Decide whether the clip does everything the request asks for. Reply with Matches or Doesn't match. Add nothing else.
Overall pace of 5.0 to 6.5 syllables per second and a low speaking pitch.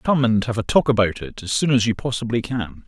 Matches